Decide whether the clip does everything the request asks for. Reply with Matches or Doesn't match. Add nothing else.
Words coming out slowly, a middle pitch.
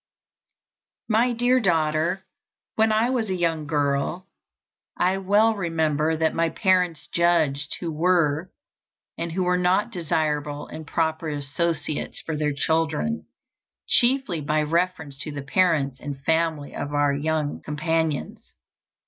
Matches